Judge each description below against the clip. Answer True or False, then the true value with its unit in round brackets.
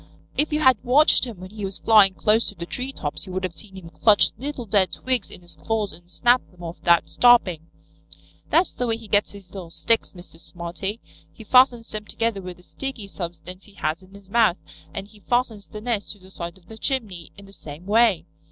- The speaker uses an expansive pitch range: False (4.2 semitones)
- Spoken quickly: True (225 wpm)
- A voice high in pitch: True (200 Hz)